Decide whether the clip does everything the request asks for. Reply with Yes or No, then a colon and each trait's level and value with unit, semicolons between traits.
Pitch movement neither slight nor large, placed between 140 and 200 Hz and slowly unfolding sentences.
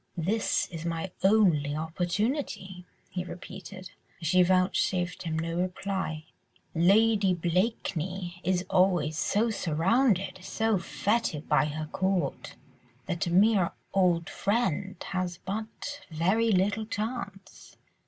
Yes: average, 3.1 semitones; medium, 185 Hz; slow, 115 wpm